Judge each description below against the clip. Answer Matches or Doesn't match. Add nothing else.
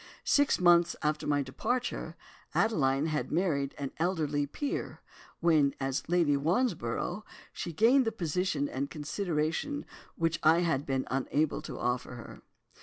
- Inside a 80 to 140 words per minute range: Matches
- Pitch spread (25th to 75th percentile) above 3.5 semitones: Matches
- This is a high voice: Doesn't match